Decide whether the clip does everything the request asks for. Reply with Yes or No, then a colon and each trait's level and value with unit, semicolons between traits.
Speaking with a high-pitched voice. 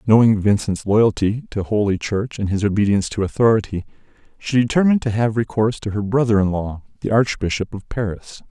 No: low, 105 Hz